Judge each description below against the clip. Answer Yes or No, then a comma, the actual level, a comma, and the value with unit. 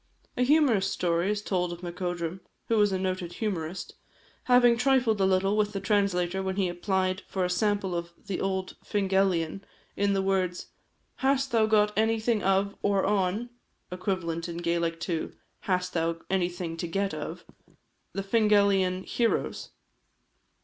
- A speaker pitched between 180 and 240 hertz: Yes, high, 190 Hz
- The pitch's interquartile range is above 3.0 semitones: No, average, 2.7 semitones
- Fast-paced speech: No, average, 150 wpm